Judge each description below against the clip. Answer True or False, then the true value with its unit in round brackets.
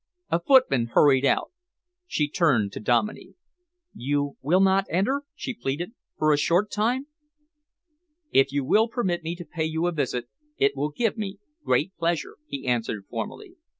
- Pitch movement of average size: False (6.8 semitones)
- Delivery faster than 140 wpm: True (160 wpm)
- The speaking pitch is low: False (165 Hz)